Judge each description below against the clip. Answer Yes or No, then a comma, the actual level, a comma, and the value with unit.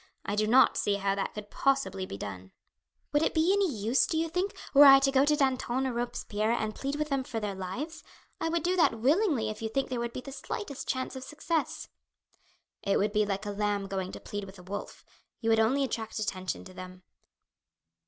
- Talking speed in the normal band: No, fast, 225 wpm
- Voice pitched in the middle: No, high, 235 Hz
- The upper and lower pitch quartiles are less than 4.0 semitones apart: No, wide, 5.4 semitones